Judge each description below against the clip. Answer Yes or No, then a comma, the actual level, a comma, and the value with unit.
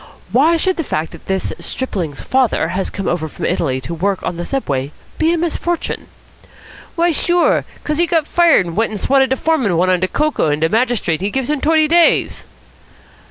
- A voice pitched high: Yes, high, 240 Hz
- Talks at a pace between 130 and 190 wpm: No, average, 200 wpm